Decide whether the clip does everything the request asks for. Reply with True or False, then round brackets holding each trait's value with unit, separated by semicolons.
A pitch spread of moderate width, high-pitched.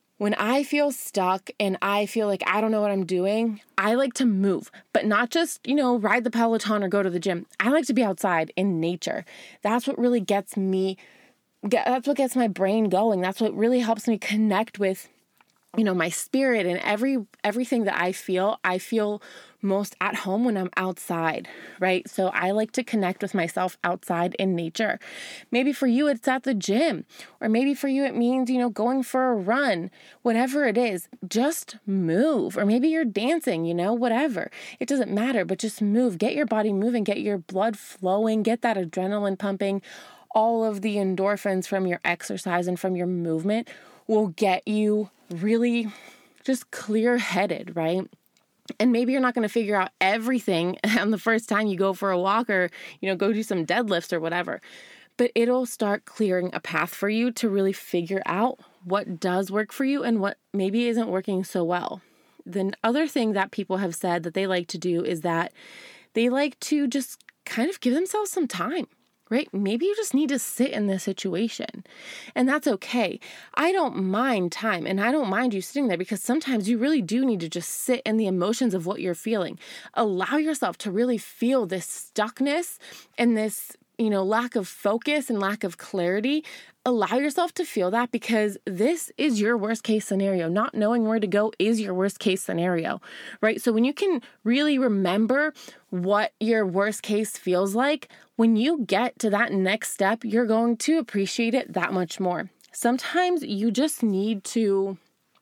True (4.3 semitones; 215 Hz)